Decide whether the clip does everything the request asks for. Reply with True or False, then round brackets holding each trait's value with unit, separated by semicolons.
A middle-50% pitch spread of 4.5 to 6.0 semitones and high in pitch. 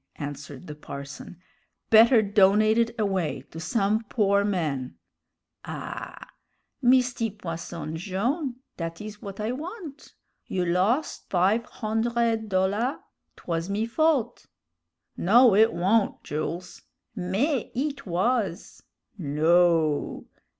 True (5.1 semitones; 200 Hz)